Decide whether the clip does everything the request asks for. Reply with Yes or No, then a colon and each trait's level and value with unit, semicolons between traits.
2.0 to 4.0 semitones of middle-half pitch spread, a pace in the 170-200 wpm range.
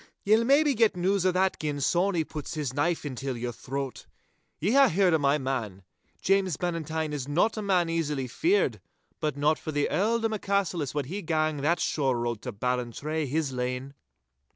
No: wide, 5.6 semitones; average, 185 wpm